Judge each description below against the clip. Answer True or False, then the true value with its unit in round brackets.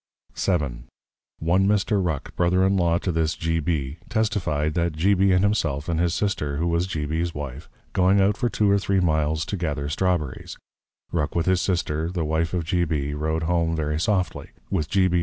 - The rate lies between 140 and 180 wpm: False (205 wpm)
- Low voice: True (85 Hz)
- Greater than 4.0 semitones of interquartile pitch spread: False (3.3 semitones)